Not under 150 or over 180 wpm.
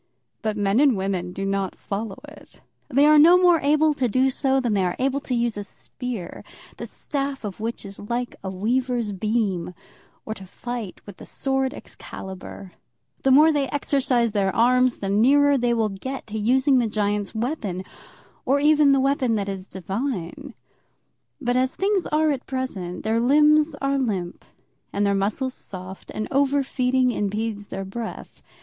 Yes: average, 170 wpm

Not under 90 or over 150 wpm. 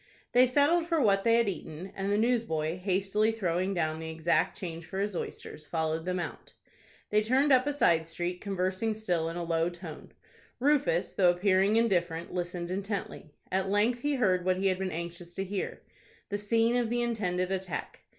No: average, 185 wpm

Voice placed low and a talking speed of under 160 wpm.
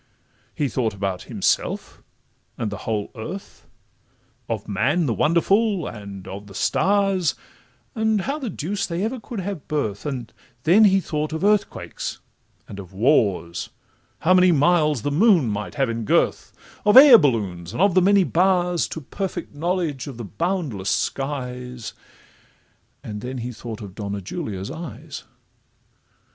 No: medium, 145 Hz; average, 150 wpm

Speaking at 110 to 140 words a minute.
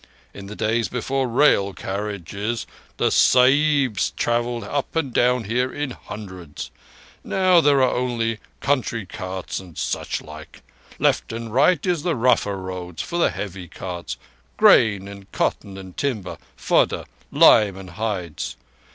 Yes: slow, 135 wpm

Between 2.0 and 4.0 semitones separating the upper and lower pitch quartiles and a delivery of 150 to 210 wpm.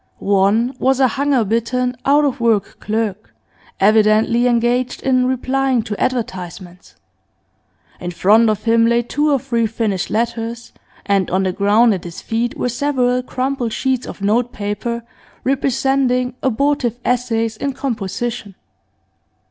No: average, 3.0 semitones; slow, 135 wpm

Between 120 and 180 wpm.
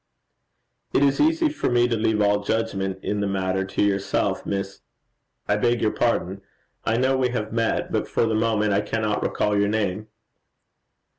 Yes: average, 175 wpm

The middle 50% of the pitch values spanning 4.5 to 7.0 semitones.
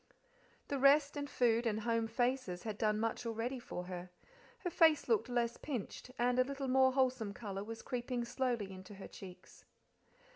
No: average, 3.5 semitones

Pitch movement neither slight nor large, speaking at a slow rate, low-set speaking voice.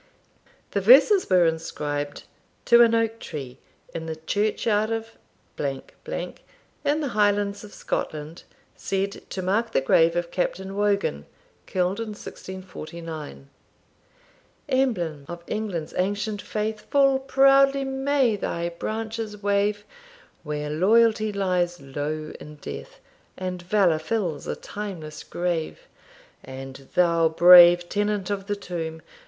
No: average, 4.9 semitones; slow, 120 wpm; high, 190 Hz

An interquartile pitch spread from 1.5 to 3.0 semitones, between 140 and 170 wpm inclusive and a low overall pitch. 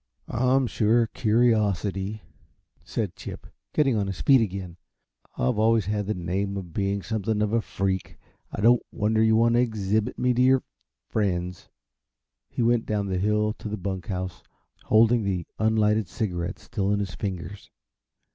Yes: average, 2.7 semitones; average, 165 wpm; low, 105 Hz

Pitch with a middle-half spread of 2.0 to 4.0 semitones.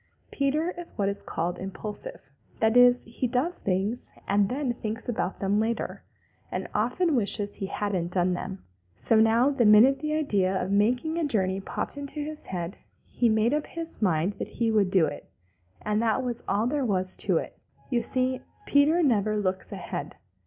No: average, 5.2 semitones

